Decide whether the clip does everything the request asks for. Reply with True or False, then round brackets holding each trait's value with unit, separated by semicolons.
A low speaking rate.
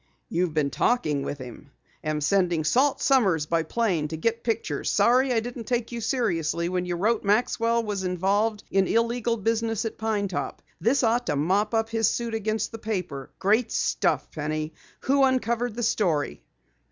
False (175 wpm)